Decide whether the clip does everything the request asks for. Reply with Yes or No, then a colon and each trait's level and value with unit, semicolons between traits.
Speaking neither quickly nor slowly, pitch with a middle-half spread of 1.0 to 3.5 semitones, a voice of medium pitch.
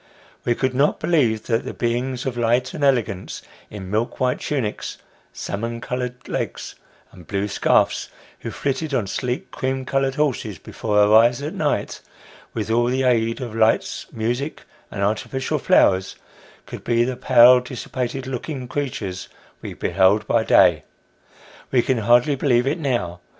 No: average, 155 wpm; average, 3.0 semitones; low, 120 Hz